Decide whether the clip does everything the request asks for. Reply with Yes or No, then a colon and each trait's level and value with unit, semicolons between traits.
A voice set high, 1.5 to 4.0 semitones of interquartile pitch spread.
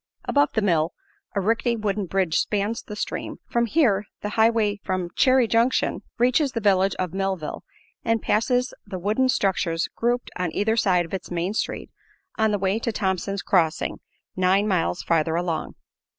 Yes: high, 200 Hz; average, 3.7 semitones